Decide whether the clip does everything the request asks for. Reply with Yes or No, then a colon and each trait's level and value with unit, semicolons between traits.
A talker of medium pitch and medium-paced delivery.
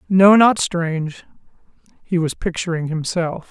No: medium, 175 Hz; slow, 105 wpm